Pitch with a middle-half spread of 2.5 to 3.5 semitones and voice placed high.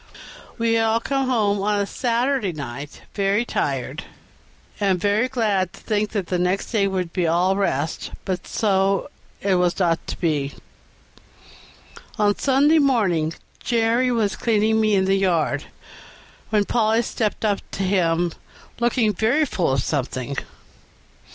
No: average, 4.1 semitones; high, 200 Hz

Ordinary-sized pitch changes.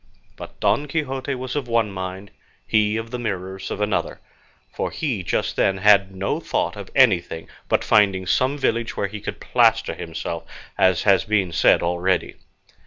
Yes: average, 3.8 semitones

